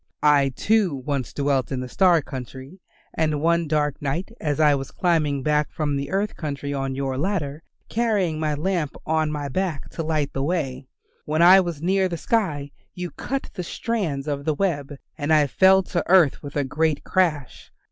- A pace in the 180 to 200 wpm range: Yes, average, 190 wpm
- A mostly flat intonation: No, average, 3.9 semitones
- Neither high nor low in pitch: Yes, medium, 150 Hz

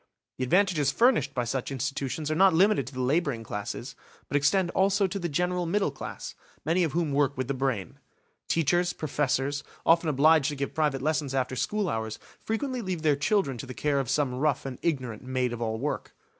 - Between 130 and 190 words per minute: No, average, 200 wpm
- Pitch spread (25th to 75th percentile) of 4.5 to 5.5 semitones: Yes, average, 4.9 semitones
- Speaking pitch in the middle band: Yes, medium, 145 Hz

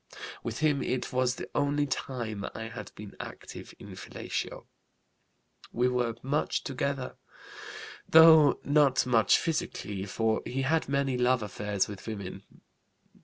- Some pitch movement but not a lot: Yes, average, 4.1 semitones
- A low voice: Yes, low, 125 Hz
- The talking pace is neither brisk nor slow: No, slow, 130 wpm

